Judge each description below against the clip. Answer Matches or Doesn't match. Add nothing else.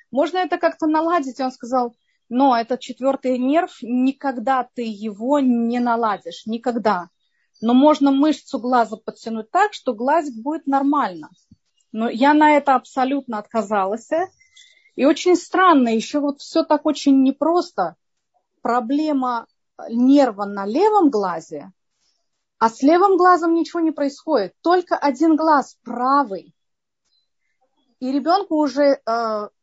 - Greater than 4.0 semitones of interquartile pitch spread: Matches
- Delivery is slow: Doesn't match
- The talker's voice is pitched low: Doesn't match